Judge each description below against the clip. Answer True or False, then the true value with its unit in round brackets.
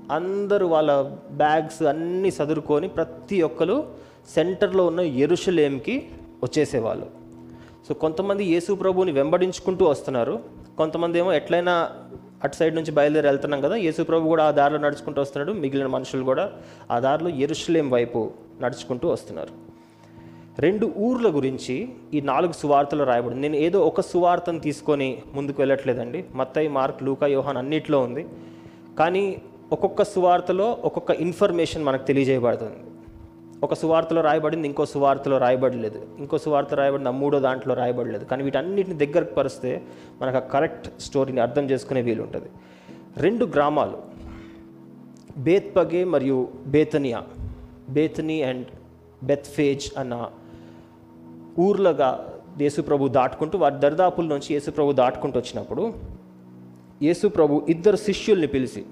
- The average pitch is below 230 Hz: True (140 Hz)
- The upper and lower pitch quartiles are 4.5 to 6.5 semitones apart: True (4.9 semitones)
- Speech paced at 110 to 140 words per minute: True (115 wpm)